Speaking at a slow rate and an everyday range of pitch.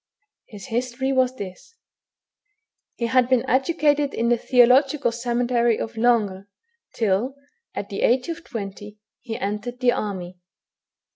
Yes: slow, 130 wpm; average, 3.6 semitones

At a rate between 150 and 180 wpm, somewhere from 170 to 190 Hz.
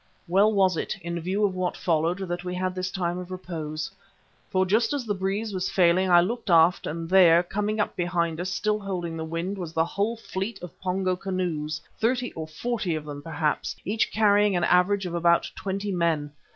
No: fast, 205 wpm; medium, 185 Hz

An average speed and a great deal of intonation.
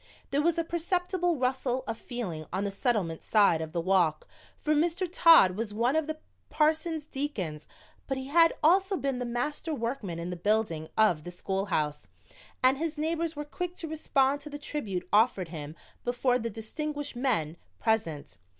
Yes: average, 175 wpm; wide, 8.1 semitones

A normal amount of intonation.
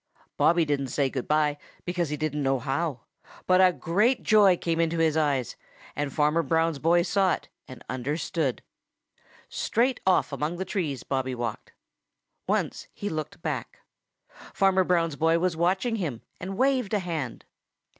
Yes: average, 4.1 semitones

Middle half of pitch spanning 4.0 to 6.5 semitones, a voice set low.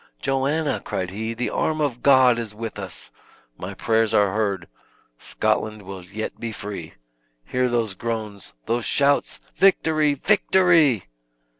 Yes: average, 5.3 semitones; low, 115 Hz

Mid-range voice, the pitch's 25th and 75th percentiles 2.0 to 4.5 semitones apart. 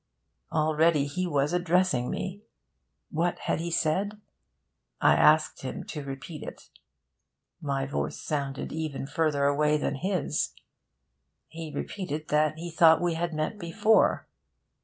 Yes: medium, 155 Hz; average, 2.9 semitones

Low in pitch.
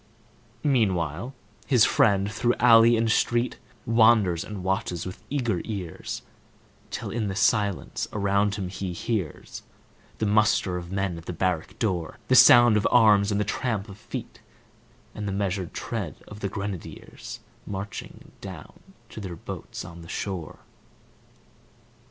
Yes: low, 100 Hz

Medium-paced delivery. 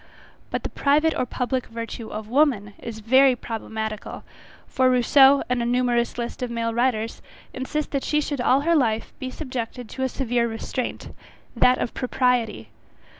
Yes: average, 165 wpm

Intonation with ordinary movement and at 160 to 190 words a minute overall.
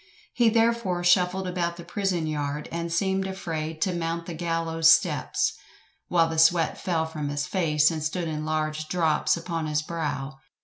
No: narrow, 2.3 semitones; average, 170 wpm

